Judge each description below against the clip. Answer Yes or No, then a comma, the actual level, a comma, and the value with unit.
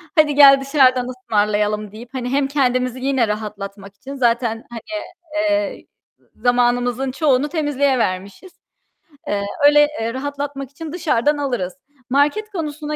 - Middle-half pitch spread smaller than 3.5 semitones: No, average, 4.0 semitones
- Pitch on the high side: Yes, very high, 260 Hz